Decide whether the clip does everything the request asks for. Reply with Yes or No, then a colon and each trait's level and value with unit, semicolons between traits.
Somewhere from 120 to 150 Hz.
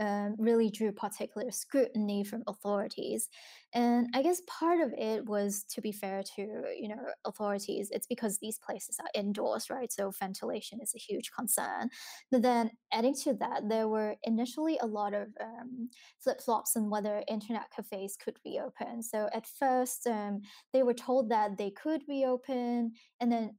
No: high, 225 Hz